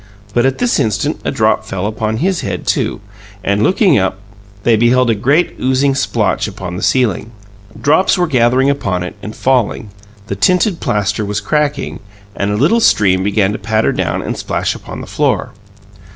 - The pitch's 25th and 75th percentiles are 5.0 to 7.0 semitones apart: Yes, wide, 5.5 semitones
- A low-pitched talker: Yes, low, 115 Hz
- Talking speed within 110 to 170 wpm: No, average, 180 wpm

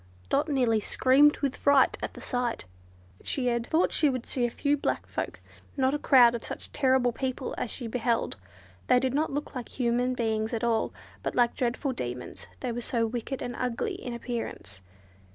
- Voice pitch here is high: Yes, high, 245 Hz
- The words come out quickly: No, average, 190 wpm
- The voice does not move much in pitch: Yes, narrow, 2.1 semitones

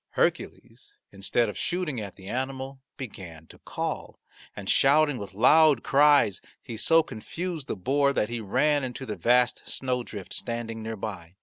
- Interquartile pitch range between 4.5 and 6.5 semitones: Yes, average, 5.1 semitones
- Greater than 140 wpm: Yes, average, 160 wpm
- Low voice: Yes, low, 125 Hz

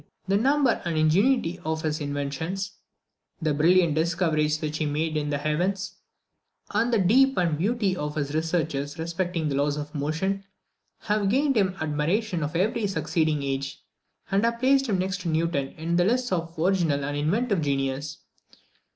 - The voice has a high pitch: No, medium, 165 Hz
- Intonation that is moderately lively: Yes, average, 4.5 semitones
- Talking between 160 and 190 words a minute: Yes, average, 170 wpm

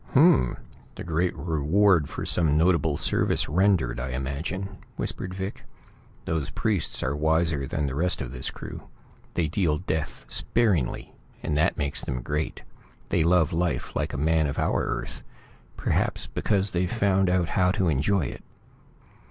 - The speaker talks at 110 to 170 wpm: Yes, average, 160 wpm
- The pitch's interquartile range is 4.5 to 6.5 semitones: No, average, 4.1 semitones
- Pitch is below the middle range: Yes, very low, 80 Hz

